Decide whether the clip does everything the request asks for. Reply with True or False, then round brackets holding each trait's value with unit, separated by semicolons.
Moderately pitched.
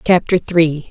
True (165 Hz)